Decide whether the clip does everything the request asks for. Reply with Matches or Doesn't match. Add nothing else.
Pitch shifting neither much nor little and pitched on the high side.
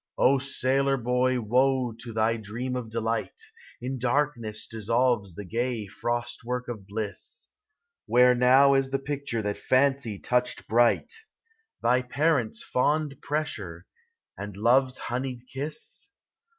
Doesn't match